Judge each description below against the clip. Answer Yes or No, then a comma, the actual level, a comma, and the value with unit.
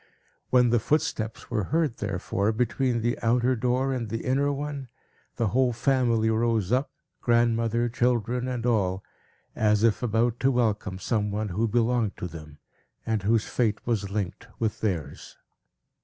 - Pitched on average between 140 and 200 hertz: No, low, 115 Hz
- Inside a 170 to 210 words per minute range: No, average, 155 wpm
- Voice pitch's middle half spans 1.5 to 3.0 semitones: Yes, average, 2.7 semitones